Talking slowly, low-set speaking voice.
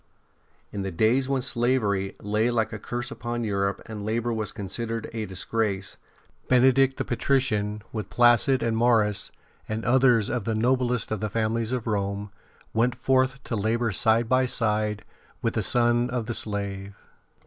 No: average, 165 wpm; low, 115 Hz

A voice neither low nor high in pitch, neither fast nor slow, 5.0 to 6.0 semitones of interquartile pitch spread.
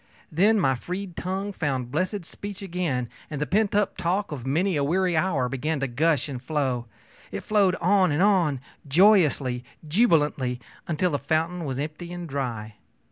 Yes: medium, 160 Hz; average, 165 wpm; wide, 5.4 semitones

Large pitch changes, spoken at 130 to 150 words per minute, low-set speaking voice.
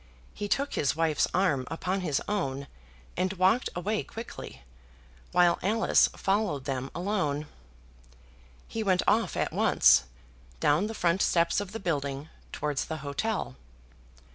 No: wide, 5.9 semitones; slow, 135 wpm; medium, 175 Hz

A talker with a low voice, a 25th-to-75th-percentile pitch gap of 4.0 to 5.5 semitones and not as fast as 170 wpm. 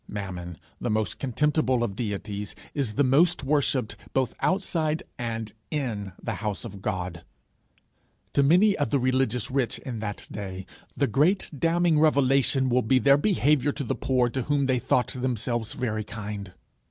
Yes: low, 125 Hz; average, 5.0 semitones; average, 160 wpm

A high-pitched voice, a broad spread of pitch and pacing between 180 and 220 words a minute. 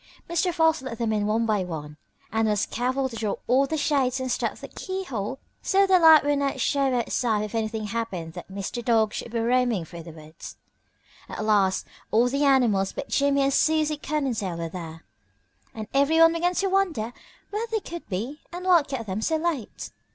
Yes: high, 245 Hz; wide, 6.4 semitones; average, 195 wpm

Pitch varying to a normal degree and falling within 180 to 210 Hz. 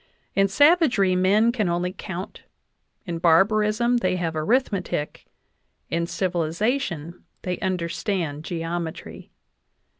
Yes: average, 4.0 semitones; medium, 185 Hz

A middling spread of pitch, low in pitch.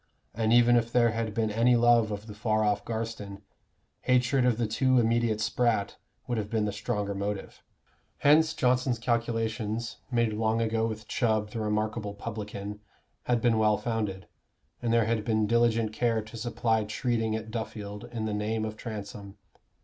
No: narrow, 1.7 semitones; low, 110 Hz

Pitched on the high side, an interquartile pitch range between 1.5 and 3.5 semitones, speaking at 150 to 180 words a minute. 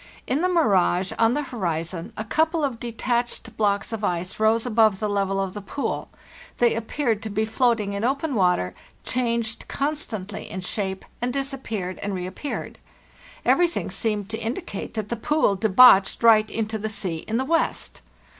No: high, 220 Hz; average, 4.0 semitones; average, 165 wpm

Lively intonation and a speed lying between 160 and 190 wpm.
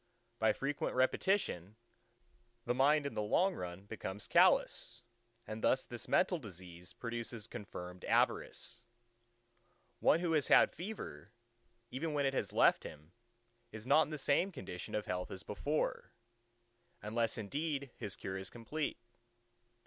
No: wide, 7.3 semitones; average, 140 wpm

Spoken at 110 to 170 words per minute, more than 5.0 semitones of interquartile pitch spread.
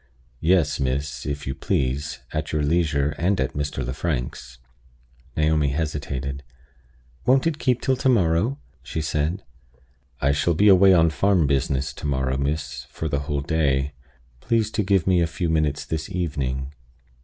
No: average, 155 wpm; average, 3.9 semitones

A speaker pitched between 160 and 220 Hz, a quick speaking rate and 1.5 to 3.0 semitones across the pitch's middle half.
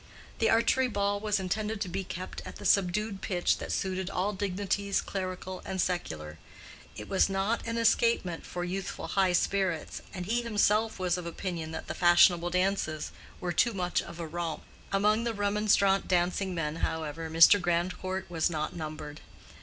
No: medium, 185 Hz; average, 170 wpm; average, 2.7 semitones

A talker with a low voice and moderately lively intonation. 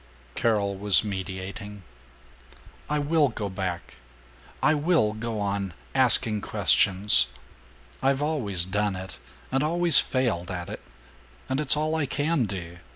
No: low, 105 Hz; wide, 6.9 semitones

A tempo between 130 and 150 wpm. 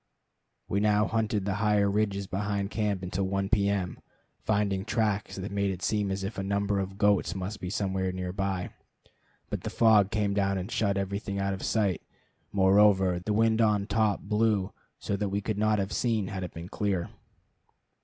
No: average, 190 wpm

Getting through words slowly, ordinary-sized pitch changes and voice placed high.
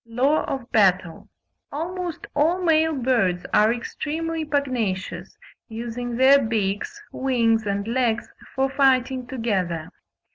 Yes: slow, 110 wpm; average, 4.3 semitones; high, 245 Hz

